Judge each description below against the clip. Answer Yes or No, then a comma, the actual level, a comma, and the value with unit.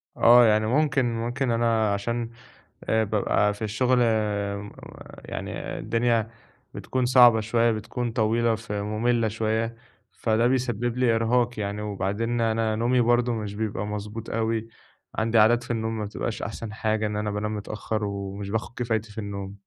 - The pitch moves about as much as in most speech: No, narrow, 1.9 semitones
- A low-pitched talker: Yes, low, 110 Hz